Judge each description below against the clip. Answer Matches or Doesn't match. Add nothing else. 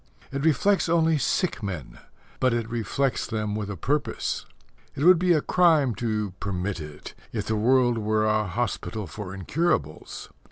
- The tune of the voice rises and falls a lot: Matches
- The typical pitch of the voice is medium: Doesn't match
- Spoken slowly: Doesn't match